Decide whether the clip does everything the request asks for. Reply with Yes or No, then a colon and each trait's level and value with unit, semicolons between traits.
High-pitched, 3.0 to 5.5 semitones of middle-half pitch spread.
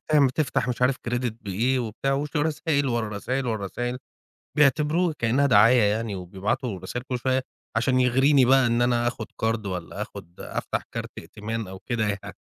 No: low, 120 Hz; average, 3.5 semitones